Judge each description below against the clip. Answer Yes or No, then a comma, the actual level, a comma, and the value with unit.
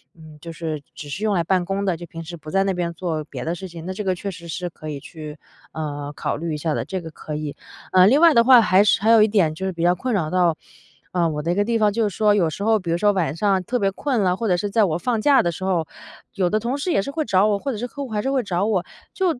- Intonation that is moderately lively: Yes, average, 4.3 semitones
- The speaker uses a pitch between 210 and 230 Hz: No, medium, 185 Hz